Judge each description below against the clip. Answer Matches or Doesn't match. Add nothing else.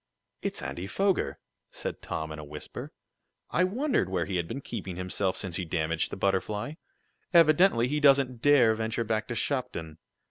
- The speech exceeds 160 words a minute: Matches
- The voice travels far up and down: Matches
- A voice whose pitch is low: Matches